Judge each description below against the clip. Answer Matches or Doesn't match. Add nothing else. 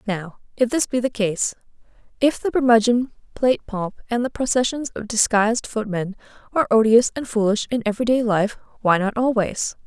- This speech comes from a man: Doesn't match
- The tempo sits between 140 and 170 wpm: Matches